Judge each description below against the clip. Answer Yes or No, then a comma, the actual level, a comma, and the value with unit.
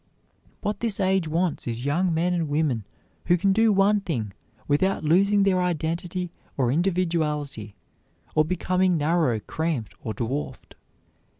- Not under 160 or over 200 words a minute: No, slow, 135 wpm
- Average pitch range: Yes, average, 4.3 semitones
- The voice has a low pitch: No, medium, 170 Hz